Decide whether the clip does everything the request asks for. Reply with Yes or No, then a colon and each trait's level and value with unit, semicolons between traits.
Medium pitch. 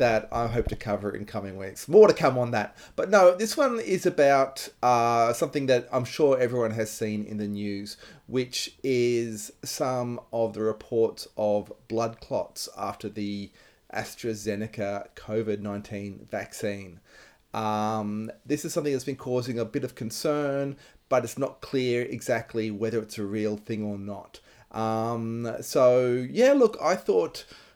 No: low, 115 Hz